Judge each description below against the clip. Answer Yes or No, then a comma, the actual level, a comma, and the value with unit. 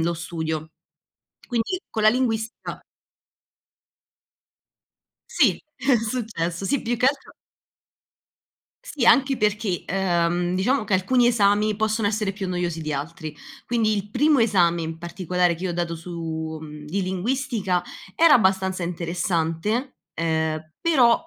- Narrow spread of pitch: No, average, 5.2 semitones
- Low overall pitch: No, high, 190 Hz